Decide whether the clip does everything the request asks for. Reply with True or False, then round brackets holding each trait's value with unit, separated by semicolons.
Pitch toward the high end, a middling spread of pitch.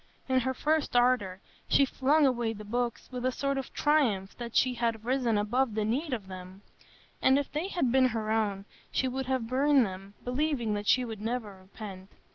True (245 Hz; 3.9 semitones)